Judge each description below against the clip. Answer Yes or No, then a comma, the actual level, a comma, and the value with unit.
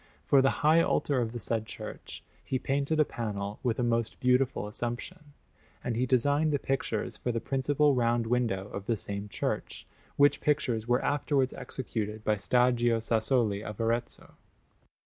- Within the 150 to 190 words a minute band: Yes, average, 160 wpm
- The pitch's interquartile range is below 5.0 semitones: Yes, average, 3.3 semitones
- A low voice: Yes, low, 120 Hz